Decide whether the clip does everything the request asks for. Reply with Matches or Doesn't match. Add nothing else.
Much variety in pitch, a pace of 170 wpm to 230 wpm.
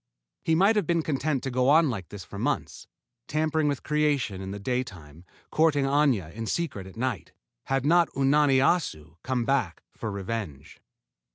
Matches